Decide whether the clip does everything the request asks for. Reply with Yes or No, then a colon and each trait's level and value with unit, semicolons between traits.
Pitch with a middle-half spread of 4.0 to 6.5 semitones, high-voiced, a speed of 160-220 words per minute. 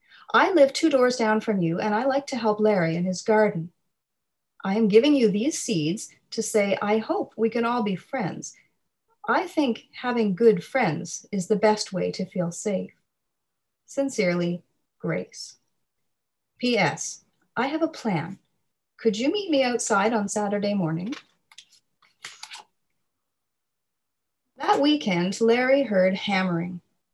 No: average, 5.0 semitones; high, 215 Hz; average, 140 wpm